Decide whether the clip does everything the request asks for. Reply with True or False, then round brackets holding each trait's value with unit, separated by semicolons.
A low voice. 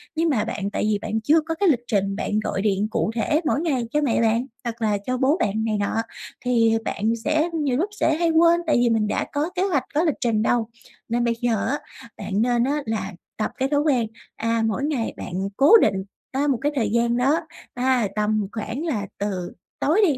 False (240 Hz)